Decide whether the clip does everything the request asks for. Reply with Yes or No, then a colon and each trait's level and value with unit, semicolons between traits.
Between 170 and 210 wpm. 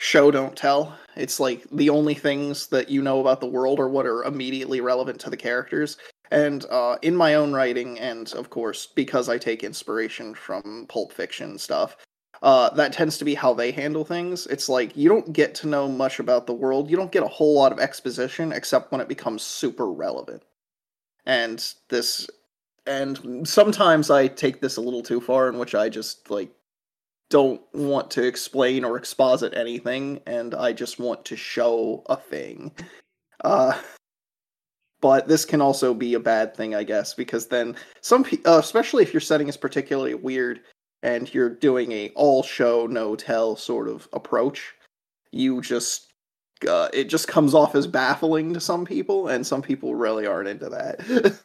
Yes: average, 185 wpm